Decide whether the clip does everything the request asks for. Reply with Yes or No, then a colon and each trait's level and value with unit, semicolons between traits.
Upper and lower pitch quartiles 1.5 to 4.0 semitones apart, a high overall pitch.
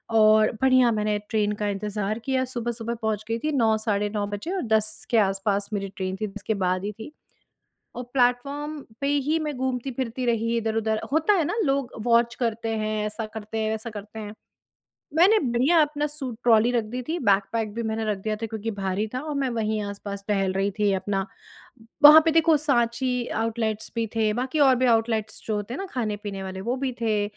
Yes: average, 3.4 semitones; high, 225 Hz